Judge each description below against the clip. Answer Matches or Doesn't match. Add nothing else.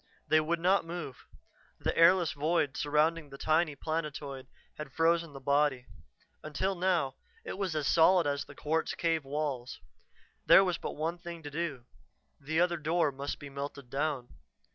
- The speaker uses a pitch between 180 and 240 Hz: Doesn't match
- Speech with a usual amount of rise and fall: Matches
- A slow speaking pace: Doesn't match